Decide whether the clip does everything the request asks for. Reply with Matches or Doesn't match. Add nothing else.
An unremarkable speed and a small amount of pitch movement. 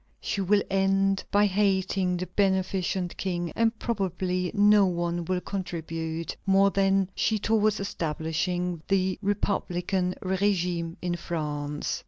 Doesn't match